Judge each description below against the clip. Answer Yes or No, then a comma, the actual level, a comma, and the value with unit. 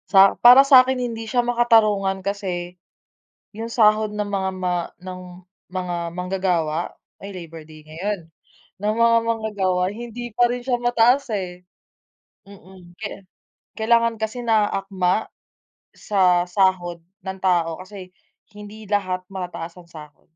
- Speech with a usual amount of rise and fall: Yes, average, 3.8 semitones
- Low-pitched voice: No, high, 195 Hz